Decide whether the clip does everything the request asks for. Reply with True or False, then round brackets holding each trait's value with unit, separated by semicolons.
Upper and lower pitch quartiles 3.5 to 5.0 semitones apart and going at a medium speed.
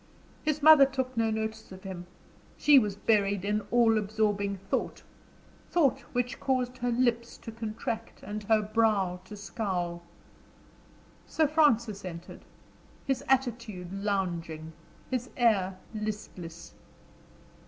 False (3.8 semitones; 120 wpm)